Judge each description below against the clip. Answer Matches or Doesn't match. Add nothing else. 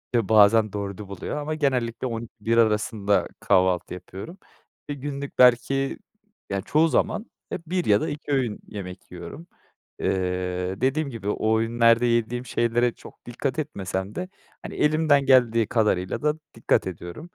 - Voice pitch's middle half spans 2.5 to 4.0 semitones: Doesn't match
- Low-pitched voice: Matches